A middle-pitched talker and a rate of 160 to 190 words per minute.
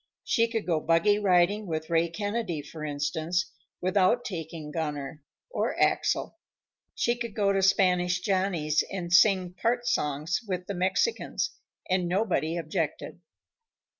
No: medium, 180 Hz; slow, 135 wpm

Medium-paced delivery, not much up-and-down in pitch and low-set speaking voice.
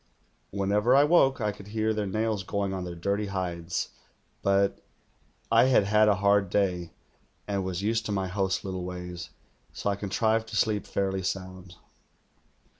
Yes: average, 165 wpm; narrow, 2.3 semitones; low, 100 Hz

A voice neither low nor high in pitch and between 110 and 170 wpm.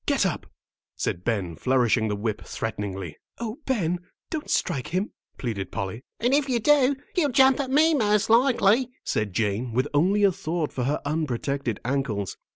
Yes: medium, 150 Hz; average, 165 wpm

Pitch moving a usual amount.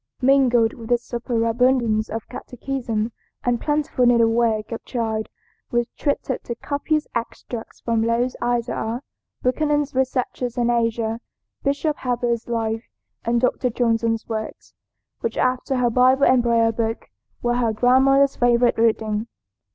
No: narrow, 1.9 semitones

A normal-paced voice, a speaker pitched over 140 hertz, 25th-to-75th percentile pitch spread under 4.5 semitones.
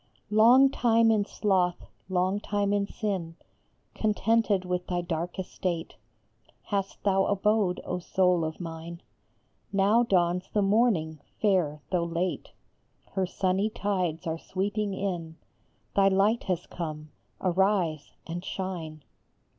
No: slow, 125 wpm; medium, 185 Hz; average, 3.1 semitones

